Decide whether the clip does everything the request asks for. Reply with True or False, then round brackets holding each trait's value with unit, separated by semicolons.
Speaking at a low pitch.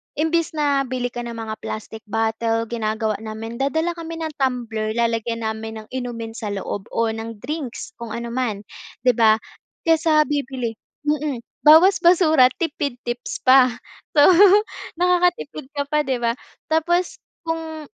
False (250 Hz)